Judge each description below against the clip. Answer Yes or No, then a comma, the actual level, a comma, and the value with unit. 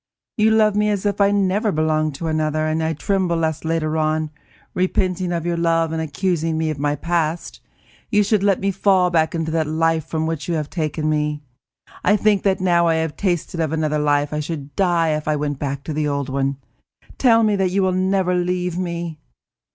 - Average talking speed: No, fast, 220 wpm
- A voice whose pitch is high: No, medium, 165 Hz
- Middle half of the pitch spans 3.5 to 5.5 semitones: No, average, 3.1 semitones